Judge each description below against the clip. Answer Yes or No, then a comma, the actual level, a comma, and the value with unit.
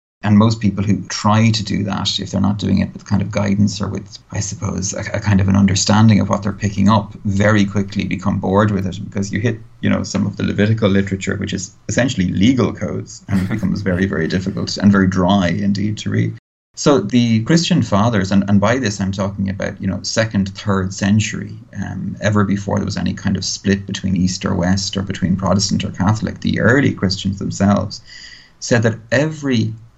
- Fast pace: Yes, fast, 215 wpm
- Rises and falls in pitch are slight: Yes, narrow, 1.3 semitones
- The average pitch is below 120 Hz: Yes, low, 100 Hz